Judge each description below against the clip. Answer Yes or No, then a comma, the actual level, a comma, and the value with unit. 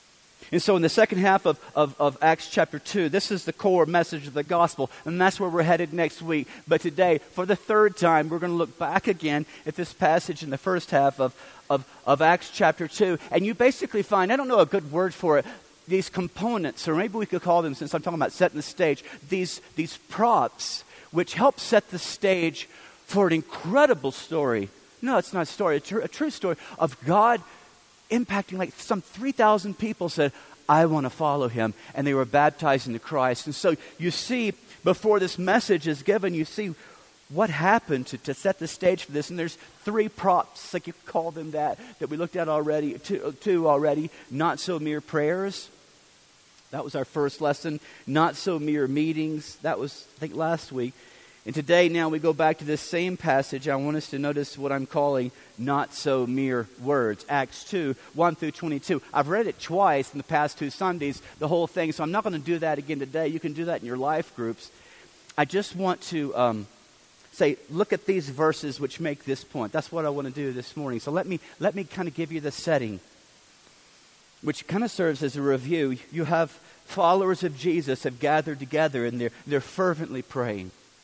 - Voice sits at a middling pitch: Yes, medium, 160 Hz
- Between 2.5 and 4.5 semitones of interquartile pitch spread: Yes, average, 4.1 semitones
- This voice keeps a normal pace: No, fast, 215 wpm